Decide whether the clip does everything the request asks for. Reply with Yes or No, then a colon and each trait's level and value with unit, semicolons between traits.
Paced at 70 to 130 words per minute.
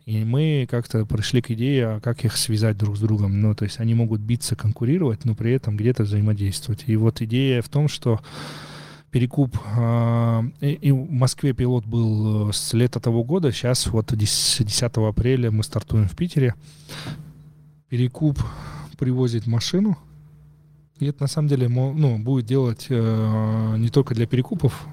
No: average, 155 wpm